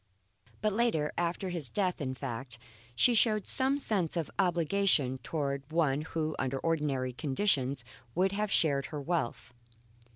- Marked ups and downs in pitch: Yes, wide, 5.9 semitones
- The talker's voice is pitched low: No, medium, 160 Hz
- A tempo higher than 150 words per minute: No, average, 140 wpm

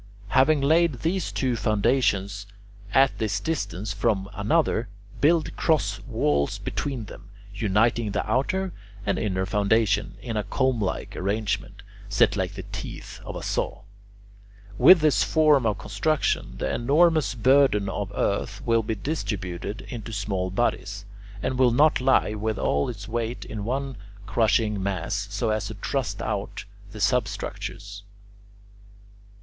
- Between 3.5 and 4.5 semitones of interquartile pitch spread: No, average, 4.9 semitones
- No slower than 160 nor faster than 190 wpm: No, average, 140 wpm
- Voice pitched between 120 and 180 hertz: No, low, 110 Hz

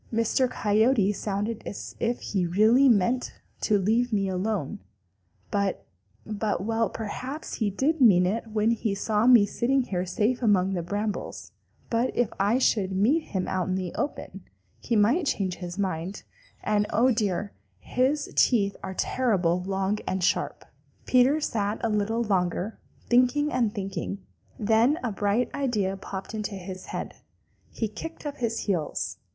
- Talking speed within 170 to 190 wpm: No, average, 155 wpm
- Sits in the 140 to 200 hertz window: No, high, 210 Hz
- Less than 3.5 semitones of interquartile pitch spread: No, average, 3.8 semitones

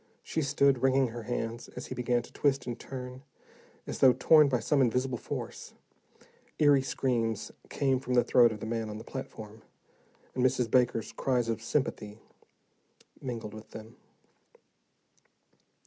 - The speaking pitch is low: Yes, low, 125 Hz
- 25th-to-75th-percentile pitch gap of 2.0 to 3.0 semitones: Yes, average, 2.7 semitones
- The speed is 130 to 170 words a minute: Yes, average, 150 wpm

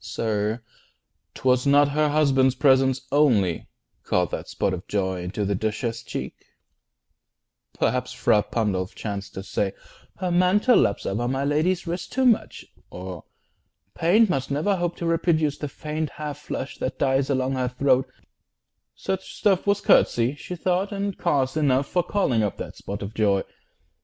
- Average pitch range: No, wide, 7.4 semitones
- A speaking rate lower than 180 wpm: Yes, average, 160 wpm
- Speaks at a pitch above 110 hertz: Yes, low, 135 Hz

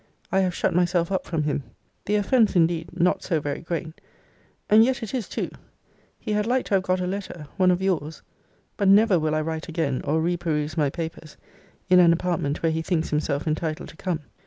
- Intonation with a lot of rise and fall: No, average, 3.2 semitones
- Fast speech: Yes, fast, 210 wpm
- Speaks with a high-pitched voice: No, medium, 170 Hz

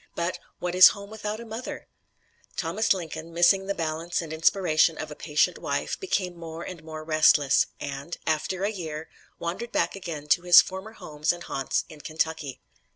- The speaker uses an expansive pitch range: No, average, 3.4 semitones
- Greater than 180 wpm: No, average, 175 wpm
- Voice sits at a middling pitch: Yes, medium, 170 Hz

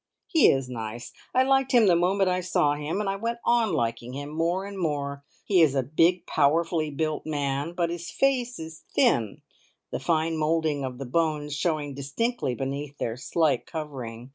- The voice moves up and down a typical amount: Yes, average, 4.5 semitones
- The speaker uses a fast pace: No, average, 185 wpm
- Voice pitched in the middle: Yes, medium, 155 Hz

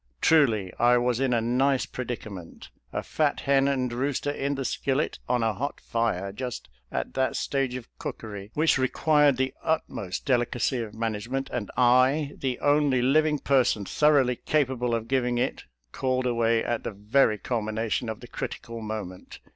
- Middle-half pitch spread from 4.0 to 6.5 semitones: No, average, 3.1 semitones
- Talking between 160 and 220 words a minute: Yes, average, 170 wpm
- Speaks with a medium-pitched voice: No, low, 125 Hz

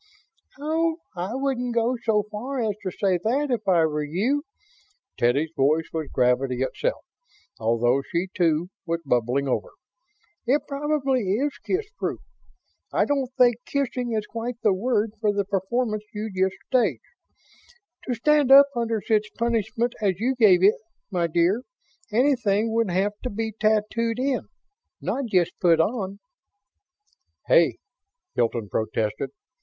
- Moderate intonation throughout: No, wide, 6.3 semitones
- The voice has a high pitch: Yes, high, 215 Hz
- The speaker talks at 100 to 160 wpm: Yes, average, 140 wpm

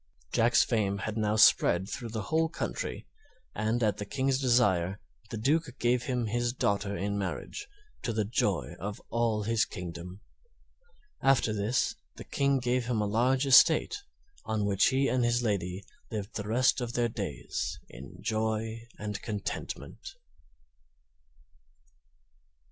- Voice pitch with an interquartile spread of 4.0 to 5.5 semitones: No, average, 3.3 semitones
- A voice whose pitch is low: Yes, low, 110 Hz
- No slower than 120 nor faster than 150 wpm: Yes, average, 145 wpm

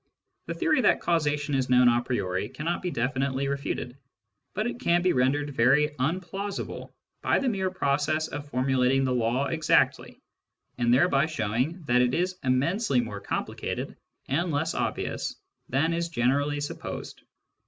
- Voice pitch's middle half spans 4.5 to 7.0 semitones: Yes, average, 4.9 semitones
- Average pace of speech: Yes, average, 150 wpm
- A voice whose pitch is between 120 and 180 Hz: Yes, medium, 140 Hz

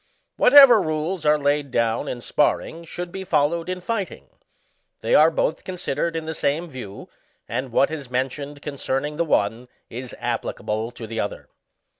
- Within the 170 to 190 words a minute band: No, average, 160 wpm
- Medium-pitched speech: Yes, medium, 150 Hz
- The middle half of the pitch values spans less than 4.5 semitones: No, average, 5.1 semitones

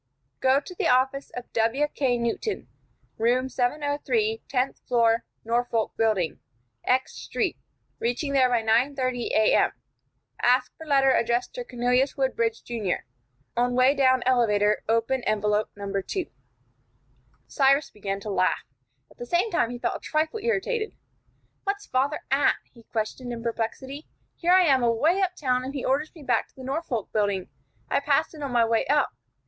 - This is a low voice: No, very high, 255 Hz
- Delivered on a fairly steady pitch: No, average, 3.8 semitones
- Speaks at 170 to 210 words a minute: No, average, 155 wpm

